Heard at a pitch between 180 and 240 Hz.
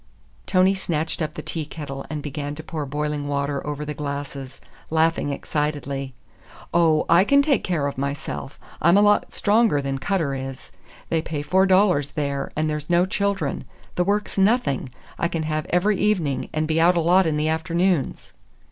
No: medium, 155 Hz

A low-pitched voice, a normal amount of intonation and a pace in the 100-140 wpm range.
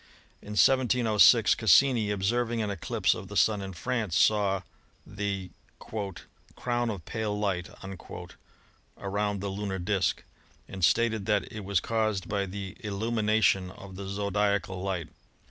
No: low, 100 Hz; narrow, 2.2 semitones; slow, 135 wpm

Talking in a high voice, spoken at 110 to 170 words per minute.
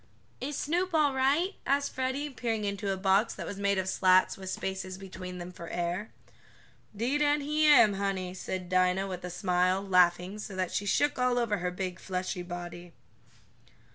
No: high, 195 Hz; average, 180 wpm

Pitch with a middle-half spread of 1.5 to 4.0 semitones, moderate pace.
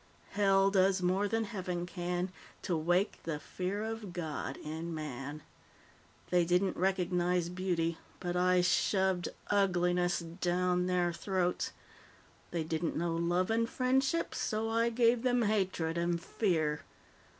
No: narrow, 2.4 semitones; slow, 130 wpm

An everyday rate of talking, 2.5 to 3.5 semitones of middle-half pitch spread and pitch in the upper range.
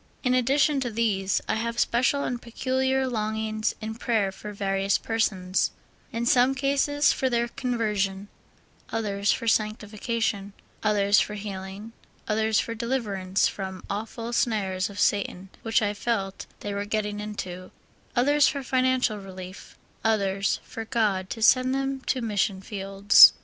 Yes: average, 145 wpm; average, 3.2 semitones; high, 215 Hz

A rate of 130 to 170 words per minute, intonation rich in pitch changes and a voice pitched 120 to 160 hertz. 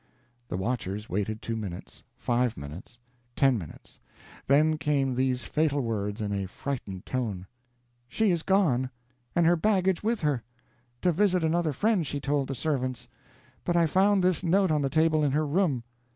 Yes: average, 165 wpm; wide, 6.2 semitones; medium, 140 Hz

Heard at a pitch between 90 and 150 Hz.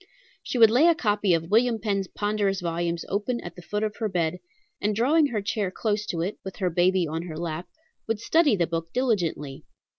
No: high, 200 Hz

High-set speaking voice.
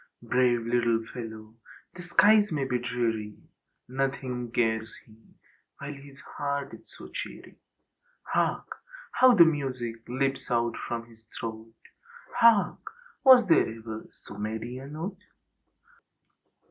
No: low, 125 Hz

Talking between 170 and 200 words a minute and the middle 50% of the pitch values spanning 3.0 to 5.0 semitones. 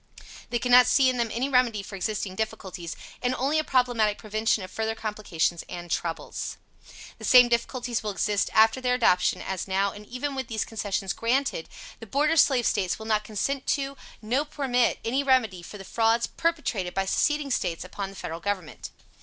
Yes: average, 185 wpm; average, 4.4 semitones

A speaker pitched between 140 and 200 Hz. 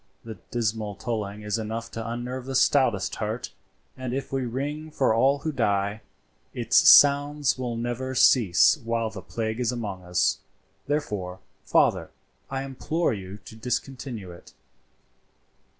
No: low, 115 Hz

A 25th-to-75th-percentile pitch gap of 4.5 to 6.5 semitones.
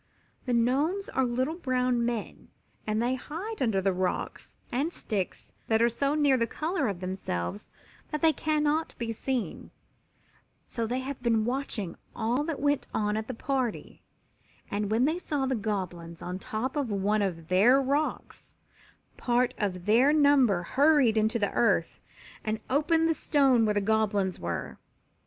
Yes: average, 5.0 semitones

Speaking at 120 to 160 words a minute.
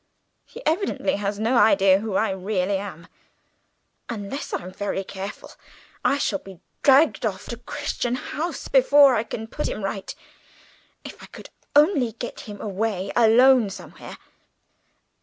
Yes: average, 140 wpm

